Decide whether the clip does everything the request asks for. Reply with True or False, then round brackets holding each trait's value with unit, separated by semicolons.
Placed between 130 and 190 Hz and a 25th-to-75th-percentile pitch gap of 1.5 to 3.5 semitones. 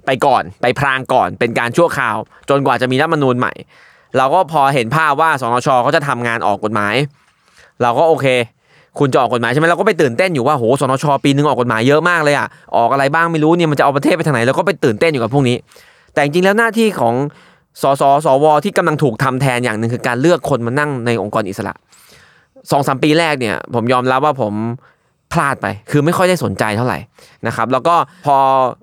False (140 Hz; 4.5 semitones)